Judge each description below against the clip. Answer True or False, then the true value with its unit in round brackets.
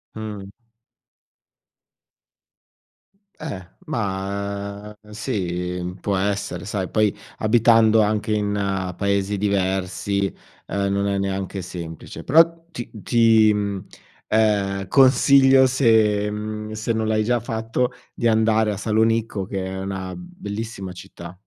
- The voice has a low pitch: True (105 Hz)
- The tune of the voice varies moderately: False (2.2 semitones)